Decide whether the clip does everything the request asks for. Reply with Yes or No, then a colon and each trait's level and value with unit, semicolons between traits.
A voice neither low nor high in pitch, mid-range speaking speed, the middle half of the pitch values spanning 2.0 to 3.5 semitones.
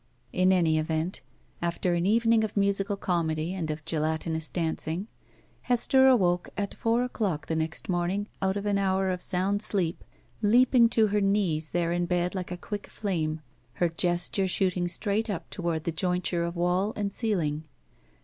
Yes: medium, 180 Hz; average, 170 wpm; average, 3.2 semitones